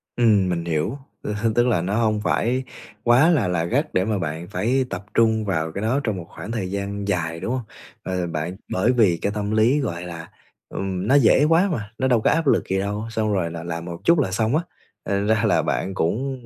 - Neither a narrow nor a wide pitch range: Yes, average, 4.9 semitones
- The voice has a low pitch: Yes, low, 105 Hz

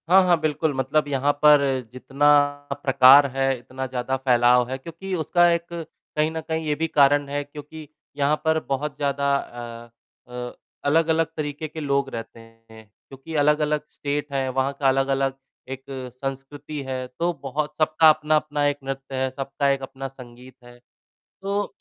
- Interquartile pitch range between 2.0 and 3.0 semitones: Yes, narrow, 2.4 semitones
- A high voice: No, medium, 140 Hz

